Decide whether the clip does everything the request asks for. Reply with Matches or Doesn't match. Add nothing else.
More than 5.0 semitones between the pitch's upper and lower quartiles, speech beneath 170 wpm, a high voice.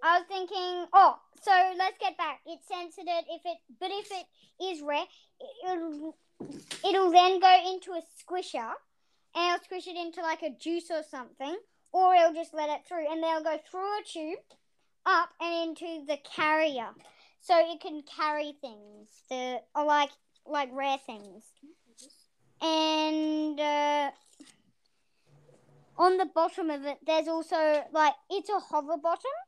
Doesn't match